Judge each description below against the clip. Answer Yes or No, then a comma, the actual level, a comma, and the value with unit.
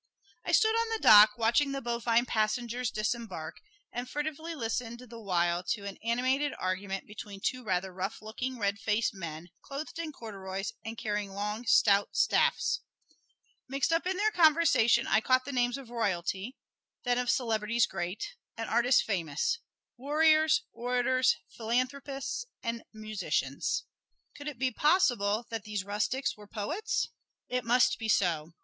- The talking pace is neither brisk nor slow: Yes, average, 150 wpm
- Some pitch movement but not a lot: Yes, average, 4.2 semitones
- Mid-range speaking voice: No, high, 235 Hz